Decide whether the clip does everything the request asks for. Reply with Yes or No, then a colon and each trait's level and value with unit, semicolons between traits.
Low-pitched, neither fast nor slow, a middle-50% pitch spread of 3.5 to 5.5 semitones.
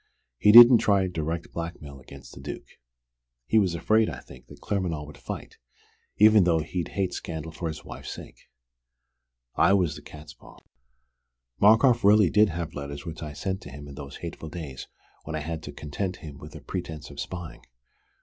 Yes: very low, 85 Hz; average, 180 wpm; average, 4.5 semitones